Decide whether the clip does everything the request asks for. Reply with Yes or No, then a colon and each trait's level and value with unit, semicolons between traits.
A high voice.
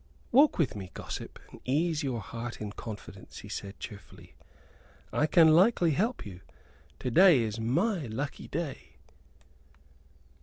No: medium, 140 Hz